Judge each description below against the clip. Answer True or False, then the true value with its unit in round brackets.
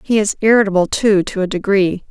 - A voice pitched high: True (200 Hz)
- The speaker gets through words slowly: False (200 wpm)